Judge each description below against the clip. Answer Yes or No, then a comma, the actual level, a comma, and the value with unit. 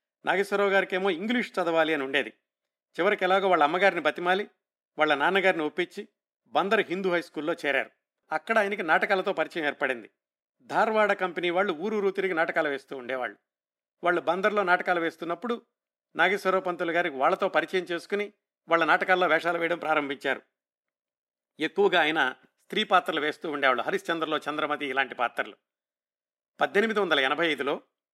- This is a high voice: No, medium, 175 Hz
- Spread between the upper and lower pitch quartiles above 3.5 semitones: Yes, average, 4.1 semitones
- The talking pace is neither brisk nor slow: No, fast, 135 wpm